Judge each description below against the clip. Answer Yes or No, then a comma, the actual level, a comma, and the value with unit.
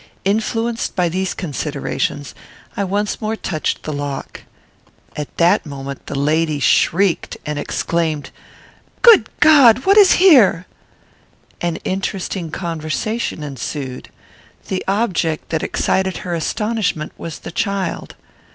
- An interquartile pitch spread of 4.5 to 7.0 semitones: Yes, average, 5.3 semitones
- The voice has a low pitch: No, medium, 175 Hz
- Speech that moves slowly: Yes, slow, 115 wpm